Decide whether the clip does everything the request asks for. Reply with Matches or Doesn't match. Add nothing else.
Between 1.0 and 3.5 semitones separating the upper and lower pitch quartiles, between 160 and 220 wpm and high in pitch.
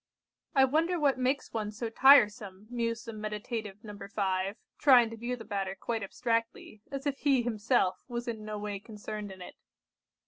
Matches